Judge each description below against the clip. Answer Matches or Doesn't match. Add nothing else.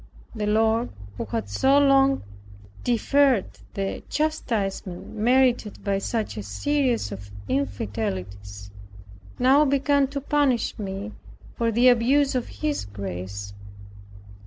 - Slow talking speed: Matches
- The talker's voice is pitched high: Matches